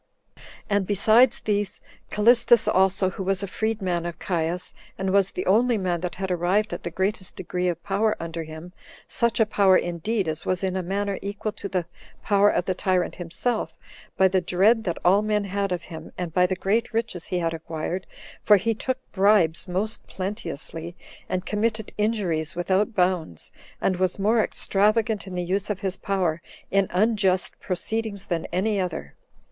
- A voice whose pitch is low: No, high, 190 Hz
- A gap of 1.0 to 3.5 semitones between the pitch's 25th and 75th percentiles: Yes, average, 2.8 semitones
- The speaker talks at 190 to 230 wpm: No, average, 180 wpm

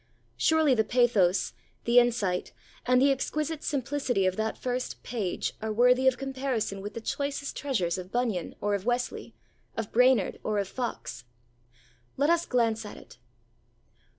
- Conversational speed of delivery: Yes, average, 150 wpm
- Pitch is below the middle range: No, high, 240 Hz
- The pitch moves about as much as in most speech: Yes, average, 4.2 semitones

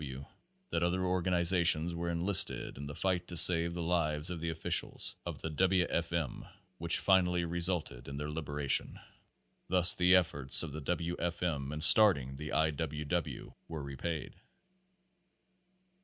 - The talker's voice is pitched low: Yes, very low, 85 Hz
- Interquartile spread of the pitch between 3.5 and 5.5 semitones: No, average, 2.8 semitones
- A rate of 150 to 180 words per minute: Yes, average, 170 wpm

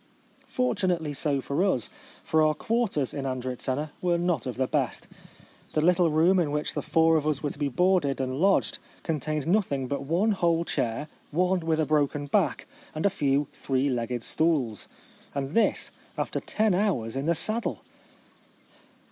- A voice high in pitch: No, medium, 155 Hz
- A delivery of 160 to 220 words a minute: Yes, average, 175 wpm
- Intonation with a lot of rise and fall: No, average, 4.3 semitones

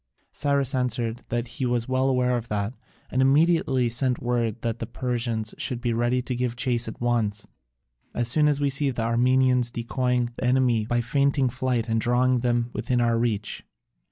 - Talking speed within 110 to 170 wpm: No, average, 185 wpm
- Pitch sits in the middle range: No, low, 120 Hz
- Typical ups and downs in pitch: No, narrow, 1.7 semitones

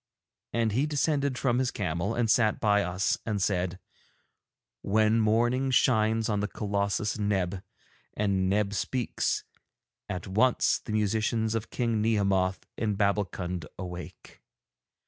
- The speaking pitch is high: No, low, 105 Hz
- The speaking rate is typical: No, slow, 125 wpm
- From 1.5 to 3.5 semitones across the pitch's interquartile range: Yes, average, 2.7 semitones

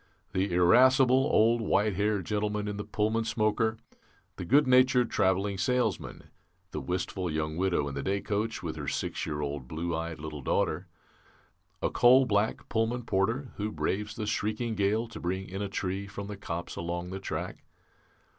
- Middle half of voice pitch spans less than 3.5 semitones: No, average, 4.1 semitones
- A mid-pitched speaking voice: No, low, 100 Hz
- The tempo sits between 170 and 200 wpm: Yes, average, 175 wpm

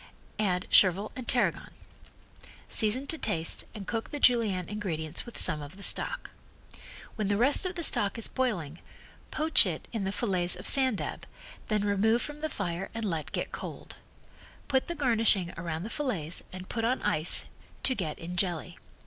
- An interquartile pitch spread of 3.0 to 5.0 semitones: No, wide, 5.6 semitones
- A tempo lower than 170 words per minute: No, average, 175 wpm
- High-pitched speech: Yes, high, 205 Hz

